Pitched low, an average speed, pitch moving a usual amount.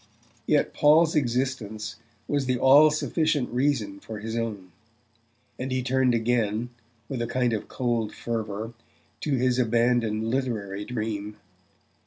No: low, 120 Hz; slow, 130 wpm; average, 3.1 semitones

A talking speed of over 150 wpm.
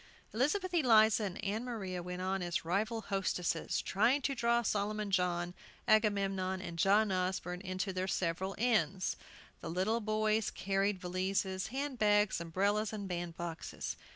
No: average, 140 wpm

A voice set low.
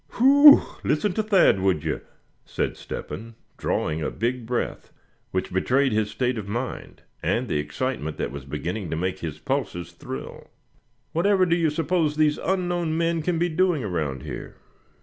Yes: low, 125 Hz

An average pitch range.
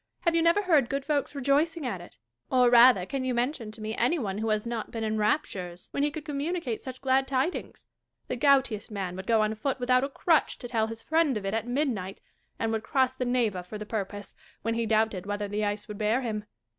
Yes: average, 4.4 semitones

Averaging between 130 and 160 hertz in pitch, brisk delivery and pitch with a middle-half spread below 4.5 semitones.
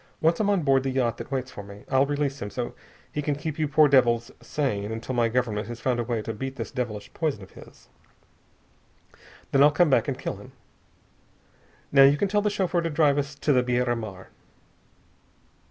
Yes: low, 135 Hz; fast, 210 wpm; average, 3.8 semitones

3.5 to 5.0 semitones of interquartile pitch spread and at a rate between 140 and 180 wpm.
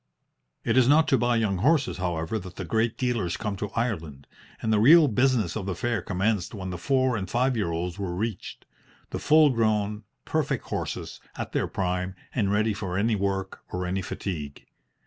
No: average, 4.3 semitones; average, 190 wpm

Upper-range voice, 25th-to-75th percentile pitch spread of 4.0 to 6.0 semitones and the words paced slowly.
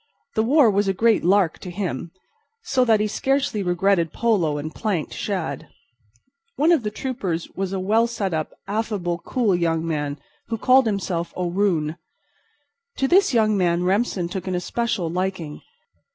No: high, 195 Hz; average, 4.6 semitones; average, 160 wpm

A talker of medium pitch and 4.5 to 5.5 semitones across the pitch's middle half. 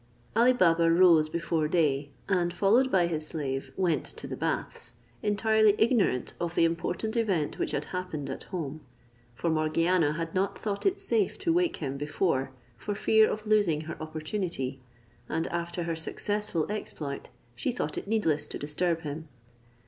Yes: medium, 170 Hz; average, 4.9 semitones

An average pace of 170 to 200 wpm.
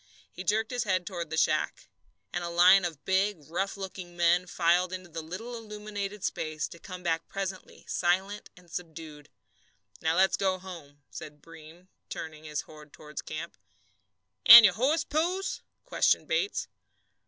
No: average, 155 wpm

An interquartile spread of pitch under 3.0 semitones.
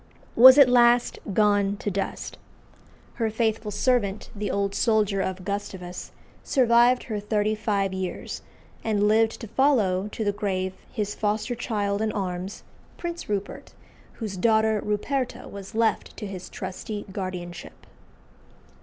Yes: narrow, 2.4 semitones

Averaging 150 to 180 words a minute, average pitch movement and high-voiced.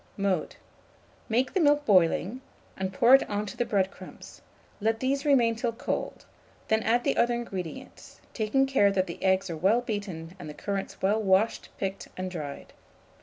Yes: average, 170 wpm; average, 4.0 semitones; high, 210 Hz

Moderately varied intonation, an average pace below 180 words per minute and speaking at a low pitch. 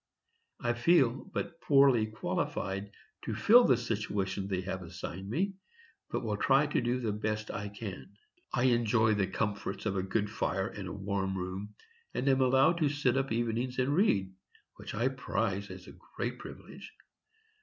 Yes: average, 4.7 semitones; average, 170 wpm; low, 110 Hz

